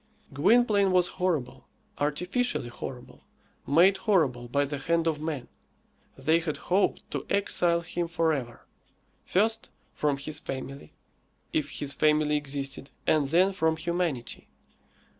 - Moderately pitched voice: Yes, medium, 155 Hz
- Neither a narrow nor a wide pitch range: Yes, average, 4.2 semitones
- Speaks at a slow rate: Yes, slow, 125 wpm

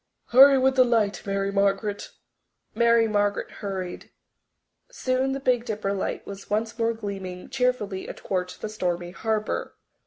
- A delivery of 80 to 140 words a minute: Yes, slow, 135 wpm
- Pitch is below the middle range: No, high, 210 Hz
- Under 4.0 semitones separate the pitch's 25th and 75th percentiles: Yes, average, 3.2 semitones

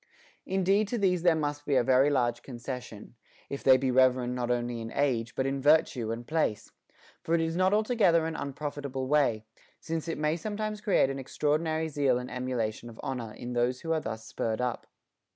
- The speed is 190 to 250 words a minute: Yes, average, 200 wpm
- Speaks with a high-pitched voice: No, low, 135 Hz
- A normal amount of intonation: Yes, average, 4.8 semitones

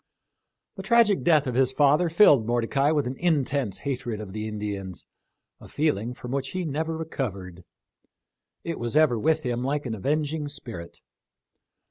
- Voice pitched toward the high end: No, low, 135 Hz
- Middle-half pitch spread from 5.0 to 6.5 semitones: Yes, average, 5.3 semitones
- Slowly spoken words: No, average, 160 wpm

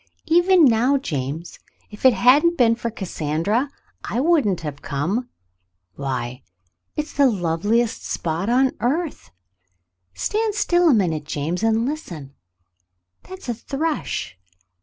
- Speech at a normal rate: No, slow, 125 wpm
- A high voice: Yes, high, 230 Hz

